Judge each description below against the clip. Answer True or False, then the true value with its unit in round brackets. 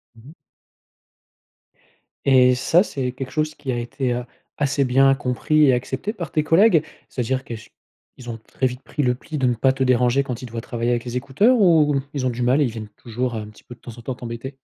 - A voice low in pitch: True (130 Hz)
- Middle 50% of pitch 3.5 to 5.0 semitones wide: False (2.7 semitones)